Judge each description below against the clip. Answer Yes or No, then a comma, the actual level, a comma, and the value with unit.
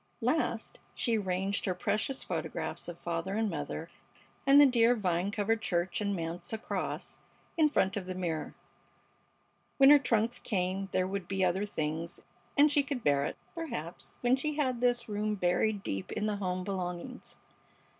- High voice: Yes, high, 200 Hz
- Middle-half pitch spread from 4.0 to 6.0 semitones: Yes, average, 5.1 semitones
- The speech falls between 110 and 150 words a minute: No, average, 165 wpm